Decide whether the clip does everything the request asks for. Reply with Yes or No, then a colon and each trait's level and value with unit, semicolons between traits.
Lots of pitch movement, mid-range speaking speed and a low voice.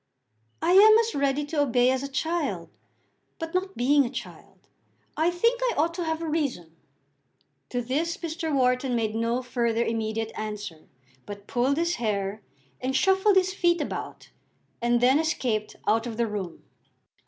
No: wide, 6.5 semitones; average, 165 wpm; very high, 265 Hz